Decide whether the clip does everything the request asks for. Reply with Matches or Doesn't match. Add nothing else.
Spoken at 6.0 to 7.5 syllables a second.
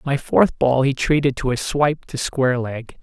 Doesn't match